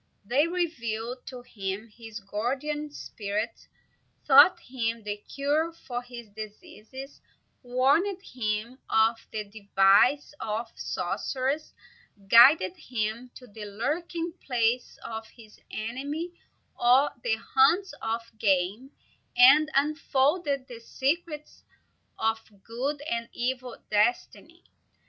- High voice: Yes, high, 245 Hz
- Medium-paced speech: No, slow, 105 wpm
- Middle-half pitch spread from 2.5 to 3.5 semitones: No, average, 4.4 semitones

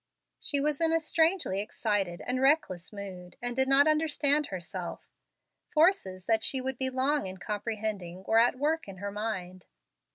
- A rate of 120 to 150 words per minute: No, average, 165 wpm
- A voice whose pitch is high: Yes, high, 225 Hz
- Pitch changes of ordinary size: No, wide, 7.2 semitones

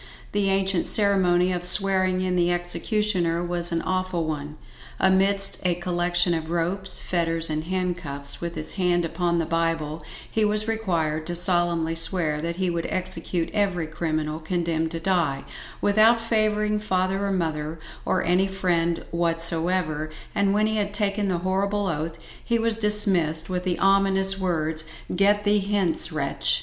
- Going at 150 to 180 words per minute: Yes, average, 155 wpm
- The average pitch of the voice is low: No, medium, 175 Hz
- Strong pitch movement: No, average, 2.9 semitones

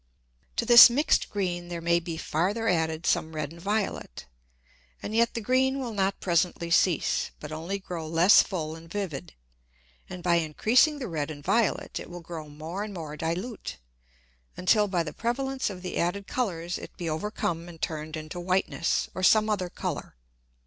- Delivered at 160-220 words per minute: Yes, average, 175 wpm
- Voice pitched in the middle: Yes, medium, 175 Hz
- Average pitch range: Yes, average, 4.3 semitones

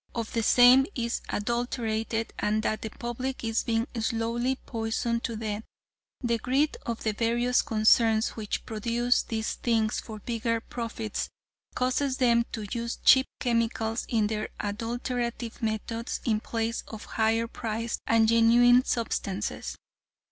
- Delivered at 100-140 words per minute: Yes, slow, 135 wpm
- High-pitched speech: Yes, high, 230 Hz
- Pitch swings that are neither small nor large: No, narrow, 1.4 semitones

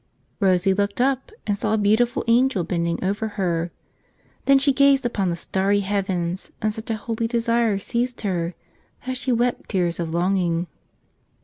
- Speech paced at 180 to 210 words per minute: No, average, 165 wpm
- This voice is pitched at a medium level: No, high, 205 Hz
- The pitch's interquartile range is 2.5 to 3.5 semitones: No, average, 4.6 semitones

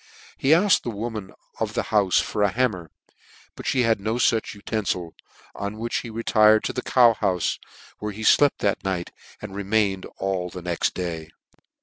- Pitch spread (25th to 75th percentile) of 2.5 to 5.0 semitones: Yes, average, 3.3 semitones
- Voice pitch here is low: Yes, low, 105 Hz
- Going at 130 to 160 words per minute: No, average, 190 wpm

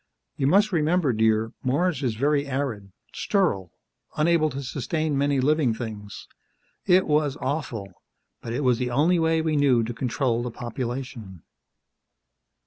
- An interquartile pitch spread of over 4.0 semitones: Yes, average, 4.7 semitones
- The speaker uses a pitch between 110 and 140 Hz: Yes, low, 135 Hz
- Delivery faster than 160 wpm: No, average, 140 wpm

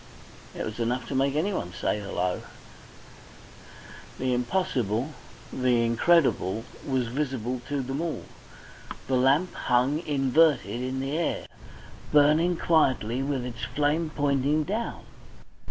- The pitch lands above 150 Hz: No, low, 135 Hz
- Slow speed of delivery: Yes, slow, 120 wpm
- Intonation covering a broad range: No, average, 3.7 semitones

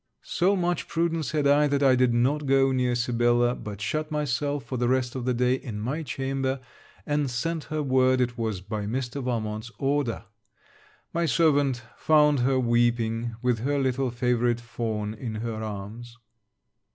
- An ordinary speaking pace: Yes, average, 165 wpm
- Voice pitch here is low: Yes, low, 125 Hz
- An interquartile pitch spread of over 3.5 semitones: No, average, 3.2 semitones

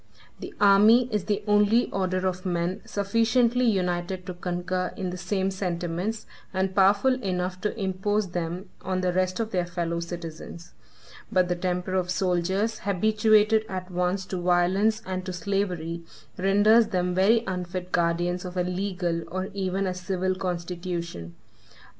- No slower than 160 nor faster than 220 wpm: No, average, 150 wpm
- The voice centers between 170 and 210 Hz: Yes, medium, 185 Hz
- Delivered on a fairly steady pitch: Yes, narrow, 2.1 semitones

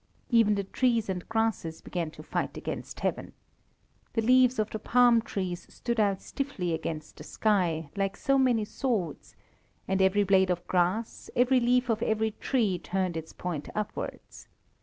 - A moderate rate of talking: Yes, average, 160 wpm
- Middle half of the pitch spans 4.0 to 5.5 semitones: Yes, average, 4.5 semitones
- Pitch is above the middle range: Yes, high, 205 Hz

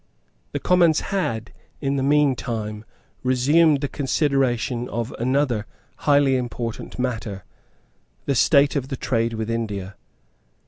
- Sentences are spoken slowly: Yes, slow, 120 wpm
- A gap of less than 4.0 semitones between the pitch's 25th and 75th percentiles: Yes, average, 3.6 semitones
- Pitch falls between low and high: No, low, 130 Hz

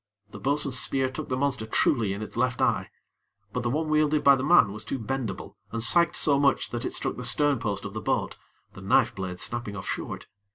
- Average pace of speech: No, fast, 230 wpm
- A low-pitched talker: Yes, low, 130 Hz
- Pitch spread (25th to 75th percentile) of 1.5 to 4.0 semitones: No, average, 4.5 semitones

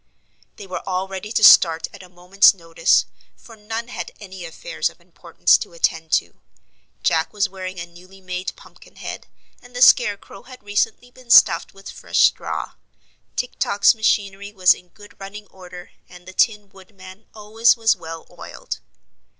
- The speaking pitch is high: Yes, high, 195 Hz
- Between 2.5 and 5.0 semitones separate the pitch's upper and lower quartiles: Yes, average, 2.8 semitones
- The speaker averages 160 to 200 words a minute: Yes, average, 165 wpm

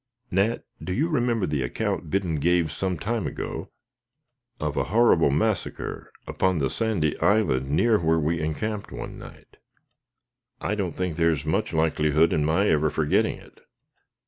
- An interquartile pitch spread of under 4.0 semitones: No, average, 5.1 semitones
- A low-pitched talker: Yes, very low, 85 Hz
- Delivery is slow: No, average, 155 wpm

